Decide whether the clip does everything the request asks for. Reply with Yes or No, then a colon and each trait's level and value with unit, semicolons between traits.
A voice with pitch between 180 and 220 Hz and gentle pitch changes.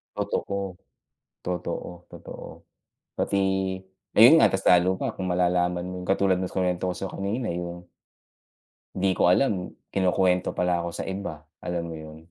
No: very low, 90 Hz; narrow, 1.5 semitones